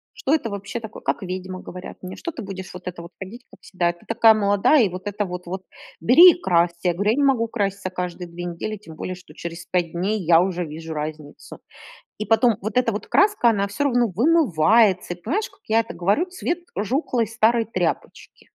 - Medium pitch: No, high, 200 Hz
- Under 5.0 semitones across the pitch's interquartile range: Yes, average, 4.5 semitones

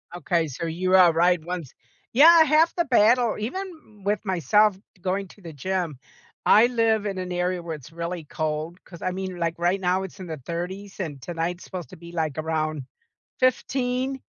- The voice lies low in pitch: No, medium, 180 Hz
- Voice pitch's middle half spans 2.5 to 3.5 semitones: No, average, 4.0 semitones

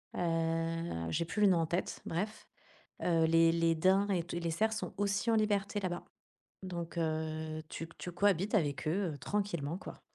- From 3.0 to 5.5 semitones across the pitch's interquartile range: Yes, average, 3.4 semitones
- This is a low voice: No, medium, 170 Hz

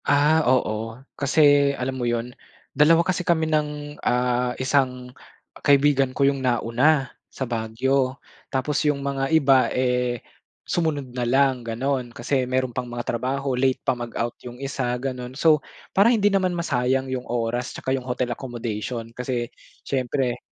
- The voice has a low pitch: Yes, low, 130 Hz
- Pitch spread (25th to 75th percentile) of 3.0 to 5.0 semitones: No, narrow, 2.5 semitones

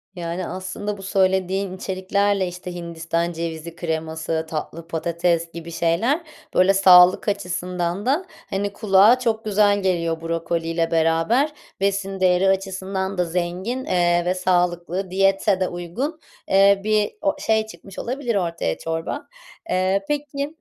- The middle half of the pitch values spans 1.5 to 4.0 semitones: Yes, average, 2.8 semitones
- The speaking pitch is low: No, medium, 185 Hz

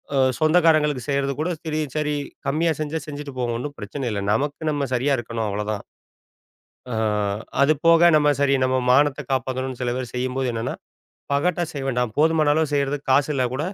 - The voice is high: No, medium, 140 Hz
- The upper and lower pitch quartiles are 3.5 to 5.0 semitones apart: No, average, 3.0 semitones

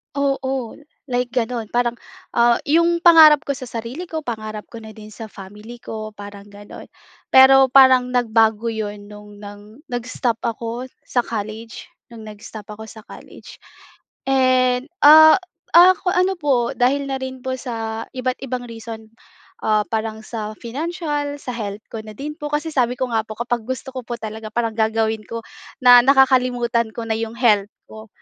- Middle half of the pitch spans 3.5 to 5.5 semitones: No, average, 3.1 semitones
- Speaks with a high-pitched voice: Yes, high, 235 Hz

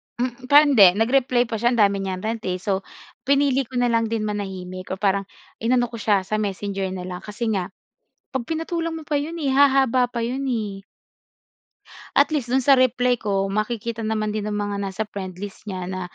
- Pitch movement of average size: Yes, average, 4.4 semitones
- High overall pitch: Yes, high, 220 Hz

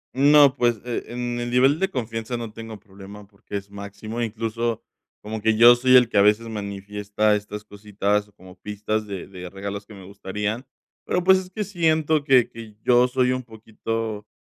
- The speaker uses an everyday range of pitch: Yes, average, 3.1 semitones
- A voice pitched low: Yes, low, 110 Hz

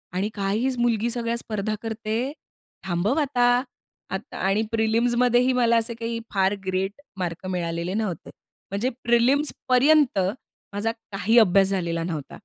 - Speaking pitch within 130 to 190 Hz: No, high, 220 Hz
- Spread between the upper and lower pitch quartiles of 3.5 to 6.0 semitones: Yes, average, 3.8 semitones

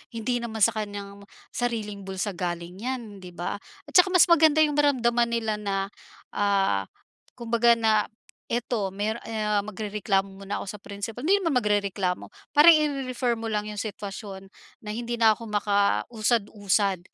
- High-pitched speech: Yes, high, 215 Hz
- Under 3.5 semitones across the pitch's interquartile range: Yes, average, 2.9 semitones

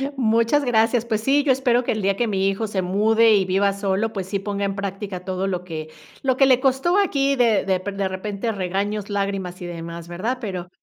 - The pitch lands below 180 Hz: No, high, 200 Hz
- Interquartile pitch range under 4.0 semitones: Yes, average, 3.6 semitones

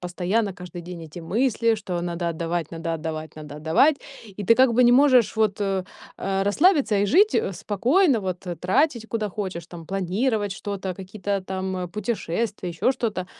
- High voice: Yes, high, 195 Hz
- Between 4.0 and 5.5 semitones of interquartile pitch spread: Yes, average, 4.4 semitones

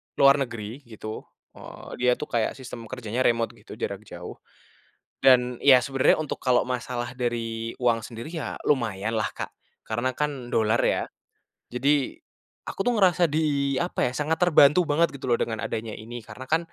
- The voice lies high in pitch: No, low, 125 Hz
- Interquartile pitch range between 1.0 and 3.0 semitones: No, average, 3.5 semitones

